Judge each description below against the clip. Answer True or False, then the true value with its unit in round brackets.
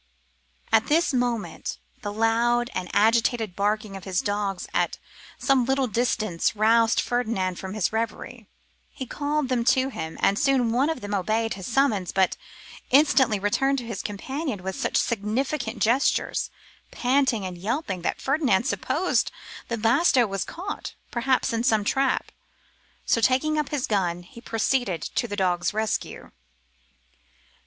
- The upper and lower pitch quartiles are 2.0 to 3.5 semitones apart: False (4.4 semitones)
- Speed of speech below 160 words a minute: True (150 wpm)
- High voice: True (230 Hz)